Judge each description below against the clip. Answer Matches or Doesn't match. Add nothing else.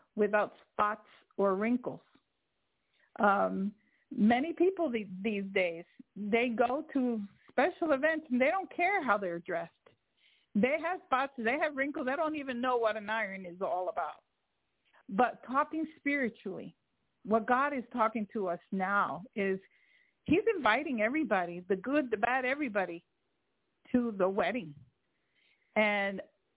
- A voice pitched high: Matches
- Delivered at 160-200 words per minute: Doesn't match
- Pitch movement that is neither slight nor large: Doesn't match